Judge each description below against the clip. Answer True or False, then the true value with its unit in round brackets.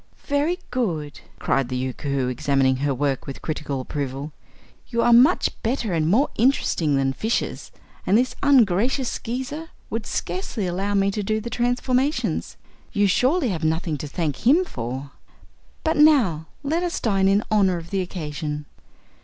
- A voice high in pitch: True (195 Hz)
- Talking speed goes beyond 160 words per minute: False (155 wpm)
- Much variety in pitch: True (9.0 semitones)